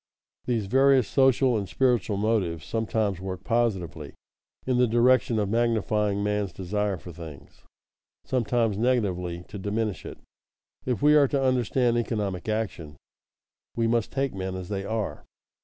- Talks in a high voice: No, low, 110 Hz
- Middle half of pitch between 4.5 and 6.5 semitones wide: No, average, 4.0 semitones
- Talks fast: No, average, 145 wpm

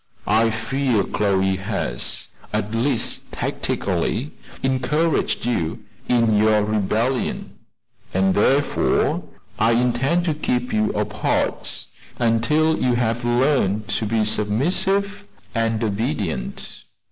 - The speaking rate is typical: No, slow, 100 wpm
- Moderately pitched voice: No, low, 115 Hz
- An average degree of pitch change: Yes, average, 3.8 semitones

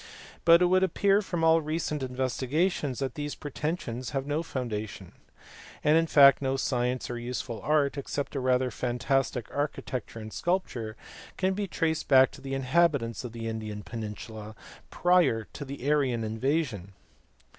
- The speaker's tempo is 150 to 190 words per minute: Yes, average, 155 wpm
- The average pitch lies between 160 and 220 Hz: No, low, 135 Hz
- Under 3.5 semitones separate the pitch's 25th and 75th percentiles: No, average, 4.7 semitones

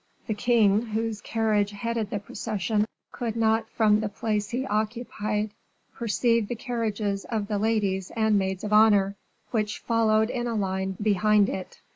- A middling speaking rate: Yes, average, 155 wpm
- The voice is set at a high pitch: Yes, high, 215 Hz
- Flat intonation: Yes, narrow, 1.8 semitones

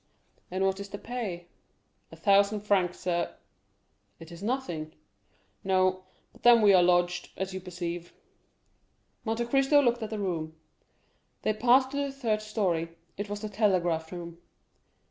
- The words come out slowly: No, average, 150 wpm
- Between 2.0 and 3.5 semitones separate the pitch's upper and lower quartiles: No, average, 3.9 semitones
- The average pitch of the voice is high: Yes, high, 195 Hz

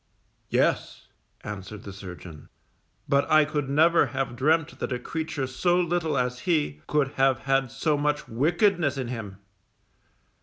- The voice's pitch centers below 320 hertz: Yes, low, 135 Hz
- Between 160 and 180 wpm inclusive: No, average, 145 wpm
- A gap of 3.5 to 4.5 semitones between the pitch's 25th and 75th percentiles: Yes, average, 4.2 semitones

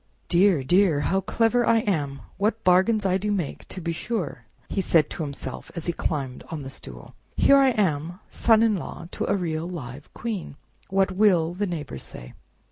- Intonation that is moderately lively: Yes, average, 4.6 semitones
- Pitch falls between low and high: Yes, medium, 180 Hz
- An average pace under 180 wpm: No, average, 195 wpm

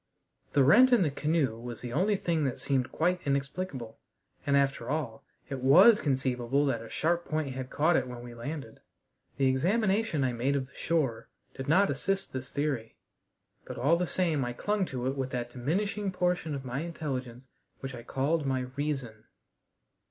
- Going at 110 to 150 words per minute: No, average, 180 wpm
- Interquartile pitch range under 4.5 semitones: No, average, 4.8 semitones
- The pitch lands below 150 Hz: Yes, medium, 140 Hz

